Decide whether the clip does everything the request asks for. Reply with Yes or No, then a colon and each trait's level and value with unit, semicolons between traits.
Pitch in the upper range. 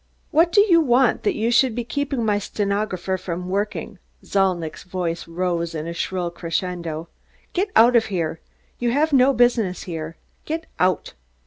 Yes: high, 195 Hz